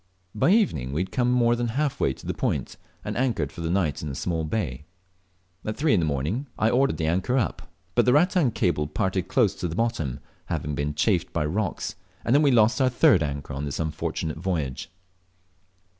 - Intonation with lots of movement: Yes, wide, 8.4 semitones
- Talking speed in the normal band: No, fast, 210 wpm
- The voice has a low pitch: Yes, very low, 95 Hz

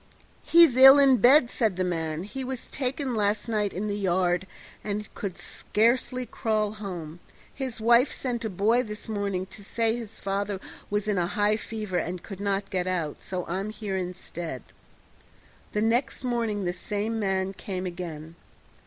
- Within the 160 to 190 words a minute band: Yes, average, 170 wpm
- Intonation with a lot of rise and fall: No, average, 3.8 semitones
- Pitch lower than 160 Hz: No, high, 205 Hz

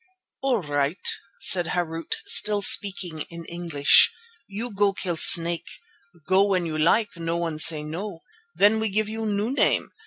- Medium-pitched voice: Yes, medium, 180 Hz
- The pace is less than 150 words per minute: No, average, 155 wpm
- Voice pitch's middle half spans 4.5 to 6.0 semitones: No, average, 3.9 semitones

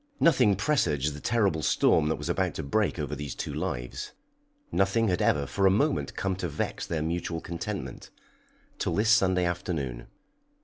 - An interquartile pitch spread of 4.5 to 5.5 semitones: Yes, average, 4.9 semitones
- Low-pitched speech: Yes, very low, 85 Hz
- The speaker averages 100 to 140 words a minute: No, average, 170 wpm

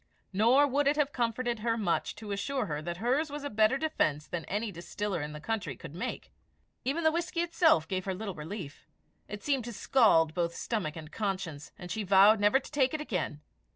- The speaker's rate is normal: No, fast, 210 wpm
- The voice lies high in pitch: Yes, high, 210 Hz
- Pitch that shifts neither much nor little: No, wide, 7.4 semitones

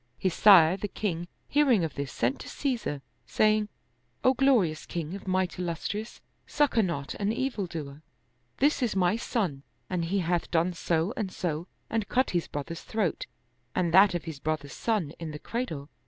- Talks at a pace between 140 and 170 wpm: No, average, 185 wpm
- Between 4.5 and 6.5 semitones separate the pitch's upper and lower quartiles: Yes, average, 5.1 semitones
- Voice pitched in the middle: Yes, medium, 180 Hz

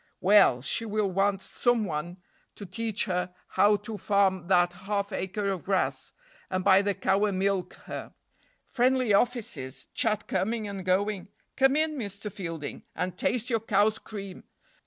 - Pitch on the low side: No, high, 200 Hz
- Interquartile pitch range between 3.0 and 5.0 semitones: No, narrow, 2.5 semitones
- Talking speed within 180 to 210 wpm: No, average, 155 wpm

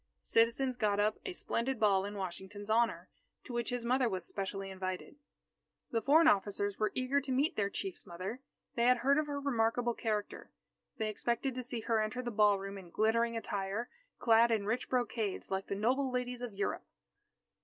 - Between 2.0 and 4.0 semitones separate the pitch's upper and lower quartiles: Yes, average, 3.6 semitones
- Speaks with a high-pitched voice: Yes, high, 225 Hz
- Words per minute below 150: No, average, 185 wpm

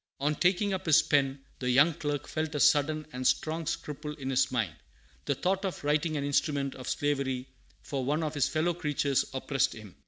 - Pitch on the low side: No, medium, 145 Hz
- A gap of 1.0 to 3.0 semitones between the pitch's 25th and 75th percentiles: Yes, average, 2.7 semitones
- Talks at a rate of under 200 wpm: No, fast, 205 wpm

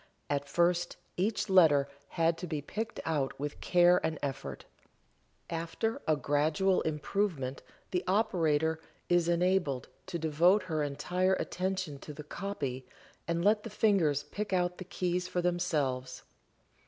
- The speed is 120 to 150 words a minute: Yes, average, 140 wpm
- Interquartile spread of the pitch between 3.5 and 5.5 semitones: Yes, average, 4.1 semitones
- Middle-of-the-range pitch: Yes, medium, 170 Hz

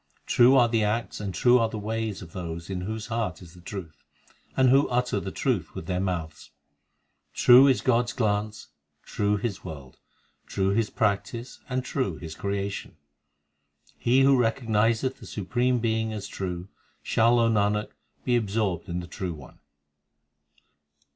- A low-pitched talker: Yes, low, 105 Hz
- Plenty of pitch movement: No, average, 4.2 semitones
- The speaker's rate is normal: Yes, average, 160 wpm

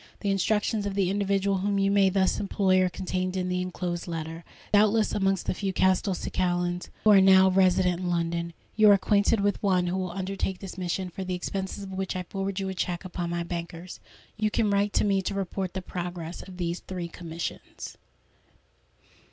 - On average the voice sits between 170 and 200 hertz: Yes, high, 190 Hz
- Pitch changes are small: Yes, narrow, 1.8 semitones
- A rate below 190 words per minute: No, average, 195 wpm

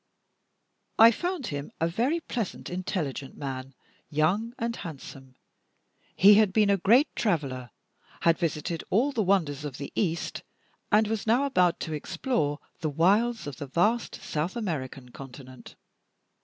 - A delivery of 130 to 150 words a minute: Yes, average, 140 wpm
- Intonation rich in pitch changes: Yes, wide, 7.4 semitones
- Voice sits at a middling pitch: Yes, medium, 175 Hz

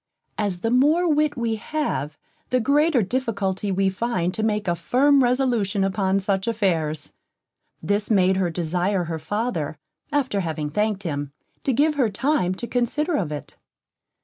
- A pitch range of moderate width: No, wide, 5.7 semitones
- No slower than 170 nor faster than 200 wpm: No, average, 155 wpm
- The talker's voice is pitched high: Yes, high, 205 Hz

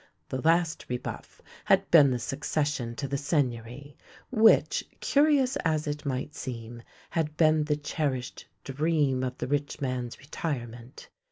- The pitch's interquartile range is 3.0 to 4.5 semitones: Yes, average, 3.5 semitones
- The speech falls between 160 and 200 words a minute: No, average, 140 wpm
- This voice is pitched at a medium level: Yes, medium, 145 Hz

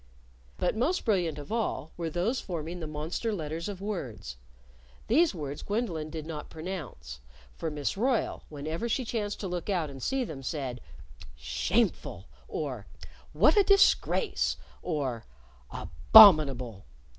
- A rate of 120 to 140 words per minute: Yes, slow, 135 wpm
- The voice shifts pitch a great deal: Yes, wide, 6.6 semitones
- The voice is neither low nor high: Yes, medium, 165 Hz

